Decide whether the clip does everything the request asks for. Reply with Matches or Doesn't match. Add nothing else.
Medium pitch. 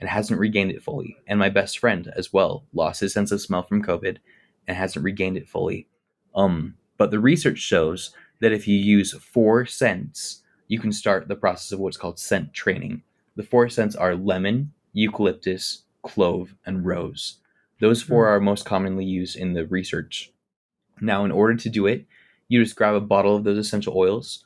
Doesn't match